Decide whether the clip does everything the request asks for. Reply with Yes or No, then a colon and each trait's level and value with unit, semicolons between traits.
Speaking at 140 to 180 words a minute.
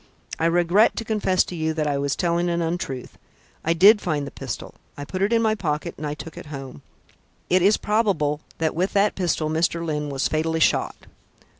No: fast, 205 wpm